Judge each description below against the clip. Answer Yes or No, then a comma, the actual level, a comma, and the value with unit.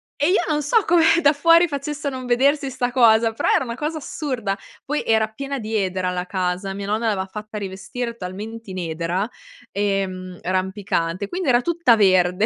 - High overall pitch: Yes, high, 220 Hz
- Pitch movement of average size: No, wide, 6.6 semitones